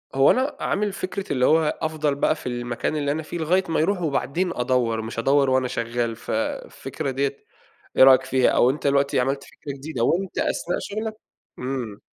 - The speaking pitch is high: No, medium, 140 Hz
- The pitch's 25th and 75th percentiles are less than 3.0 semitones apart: No, average, 4.2 semitones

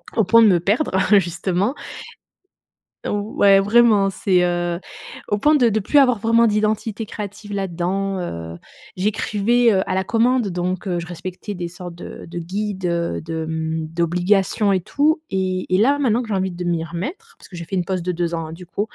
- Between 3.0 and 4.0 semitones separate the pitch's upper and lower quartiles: Yes, average, 3.6 semitones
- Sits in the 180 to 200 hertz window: Yes, high, 190 Hz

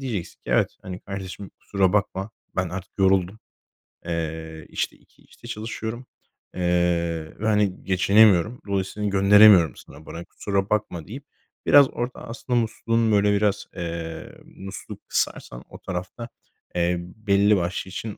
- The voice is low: Yes, very low, 95 Hz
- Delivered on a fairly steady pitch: No, average, 3.4 semitones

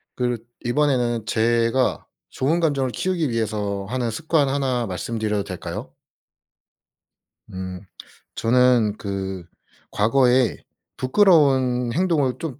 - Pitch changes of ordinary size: Yes, average, 3.9 semitones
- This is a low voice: Yes, low, 125 Hz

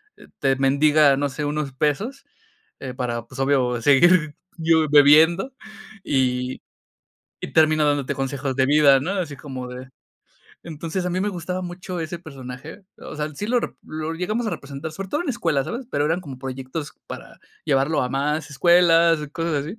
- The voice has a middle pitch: Yes, medium, 150 Hz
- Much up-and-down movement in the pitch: No, average, 4.0 semitones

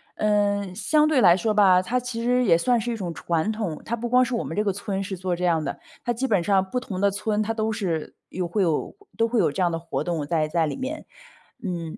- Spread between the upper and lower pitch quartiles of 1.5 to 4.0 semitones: No, average, 4.7 semitones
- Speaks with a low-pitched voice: No, high, 200 Hz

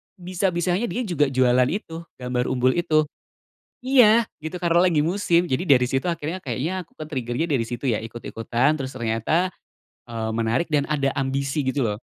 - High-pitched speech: No, medium, 145 Hz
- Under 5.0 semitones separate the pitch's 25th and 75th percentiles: No, wide, 5.6 semitones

